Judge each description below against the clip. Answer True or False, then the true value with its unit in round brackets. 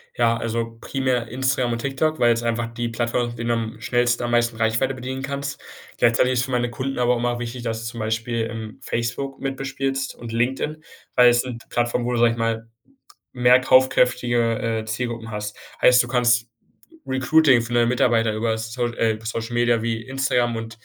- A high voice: False (120 Hz)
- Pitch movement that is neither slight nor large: False (1.6 semitones)